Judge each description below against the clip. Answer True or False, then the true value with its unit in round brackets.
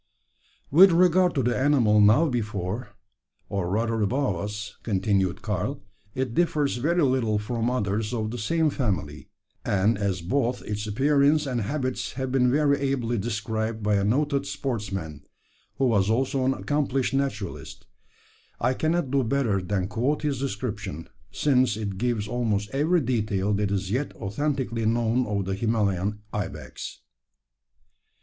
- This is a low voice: True (115 Hz)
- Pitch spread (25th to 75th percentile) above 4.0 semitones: True (4.7 semitones)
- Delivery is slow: False (145 wpm)